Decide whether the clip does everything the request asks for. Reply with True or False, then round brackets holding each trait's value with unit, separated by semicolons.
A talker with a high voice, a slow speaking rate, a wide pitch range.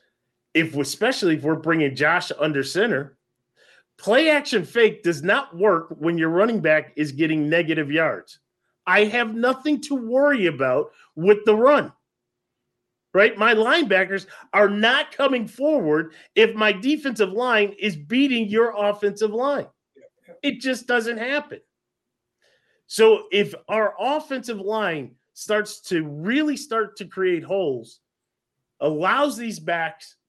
True (210 Hz; 130 wpm; 7.4 semitones)